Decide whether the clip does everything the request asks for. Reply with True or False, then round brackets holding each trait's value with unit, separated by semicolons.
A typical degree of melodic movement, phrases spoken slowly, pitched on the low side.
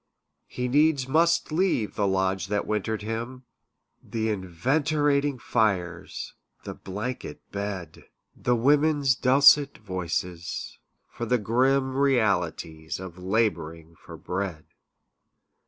False (6.3 semitones; 105 wpm; 110 Hz)